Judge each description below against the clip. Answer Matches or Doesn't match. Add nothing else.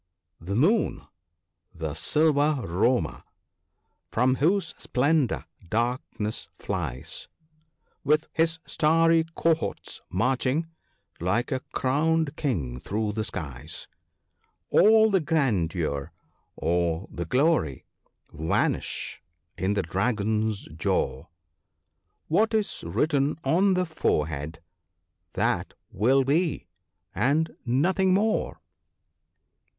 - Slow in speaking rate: Matches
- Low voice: Matches